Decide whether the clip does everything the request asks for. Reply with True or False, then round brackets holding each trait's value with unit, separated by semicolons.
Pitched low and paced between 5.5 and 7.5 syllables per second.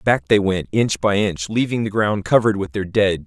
False (100 Hz; 5.2 syllables/s)